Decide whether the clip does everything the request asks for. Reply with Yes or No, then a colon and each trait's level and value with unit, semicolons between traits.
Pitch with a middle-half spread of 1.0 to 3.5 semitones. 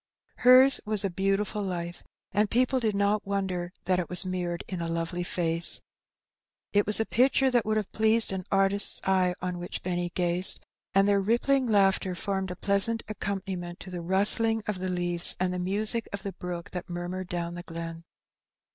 Yes: average, 2.9 semitones